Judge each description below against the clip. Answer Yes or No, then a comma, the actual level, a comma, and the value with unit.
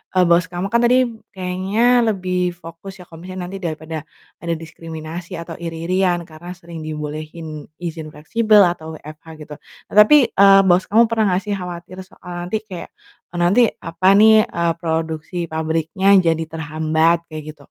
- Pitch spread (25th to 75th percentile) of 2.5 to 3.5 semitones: Yes, average, 3.1 semitones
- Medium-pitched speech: Yes, medium, 175 Hz